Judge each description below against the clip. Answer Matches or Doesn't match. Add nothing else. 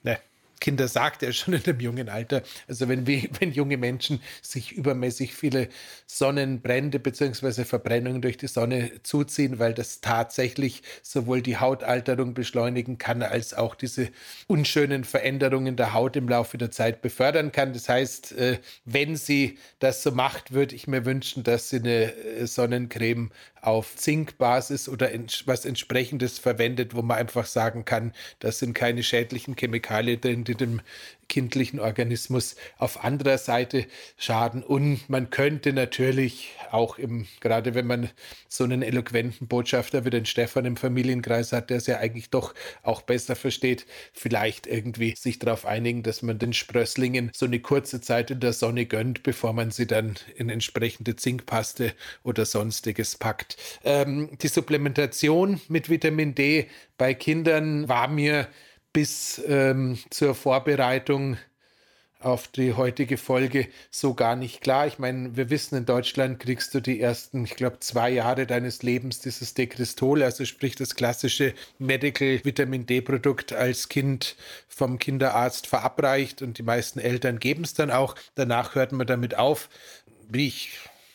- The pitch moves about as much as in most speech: Doesn't match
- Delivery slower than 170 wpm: Matches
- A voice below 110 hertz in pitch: Doesn't match